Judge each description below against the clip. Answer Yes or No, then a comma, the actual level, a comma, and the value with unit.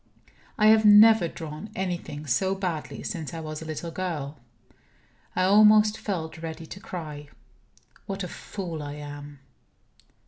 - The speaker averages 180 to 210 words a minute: No, average, 140 wpm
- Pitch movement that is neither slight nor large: Yes, average, 4.3 semitones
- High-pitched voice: No, medium, 165 Hz